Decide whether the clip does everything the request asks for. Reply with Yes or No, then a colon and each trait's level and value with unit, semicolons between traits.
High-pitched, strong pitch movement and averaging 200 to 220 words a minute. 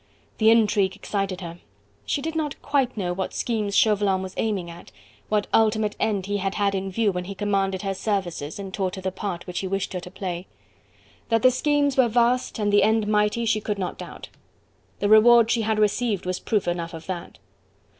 No: high, 205 Hz; average, 2.8 semitones; fast, 205 wpm